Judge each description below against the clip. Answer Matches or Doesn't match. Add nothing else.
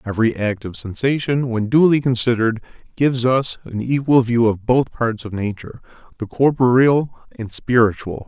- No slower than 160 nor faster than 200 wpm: Doesn't match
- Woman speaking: Doesn't match